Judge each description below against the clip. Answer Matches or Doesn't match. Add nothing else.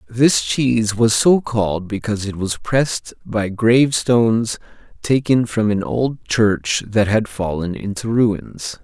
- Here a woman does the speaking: Doesn't match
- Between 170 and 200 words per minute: Doesn't match